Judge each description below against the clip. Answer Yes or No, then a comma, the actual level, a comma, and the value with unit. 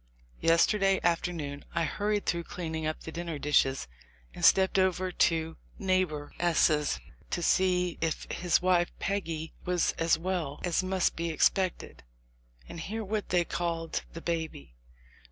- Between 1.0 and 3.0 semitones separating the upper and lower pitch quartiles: Yes, narrow, 2.4 semitones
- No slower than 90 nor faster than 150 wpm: Yes, average, 140 wpm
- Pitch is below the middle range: No, medium, 170 Hz